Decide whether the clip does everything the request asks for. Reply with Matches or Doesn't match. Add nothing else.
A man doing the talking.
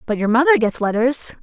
Doesn't match